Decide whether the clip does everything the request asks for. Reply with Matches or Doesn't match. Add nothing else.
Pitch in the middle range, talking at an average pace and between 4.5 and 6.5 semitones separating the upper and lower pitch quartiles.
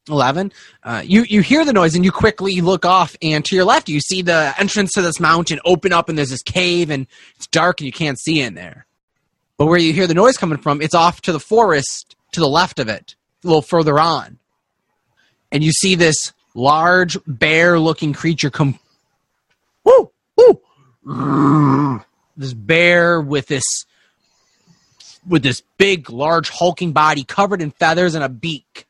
Doesn't match